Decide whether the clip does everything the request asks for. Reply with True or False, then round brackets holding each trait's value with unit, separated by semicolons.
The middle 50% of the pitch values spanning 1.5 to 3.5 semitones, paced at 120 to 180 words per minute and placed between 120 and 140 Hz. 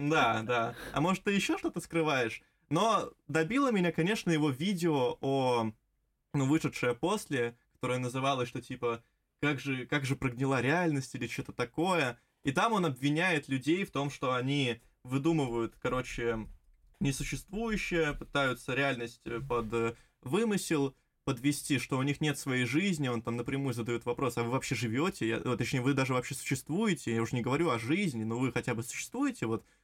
False (4.5 semitones; 160 wpm; 135 Hz)